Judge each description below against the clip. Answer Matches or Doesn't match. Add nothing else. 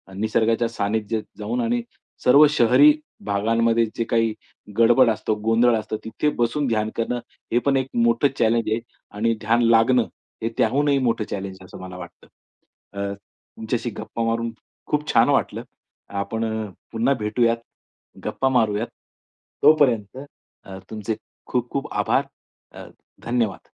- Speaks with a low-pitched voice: Matches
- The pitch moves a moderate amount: Doesn't match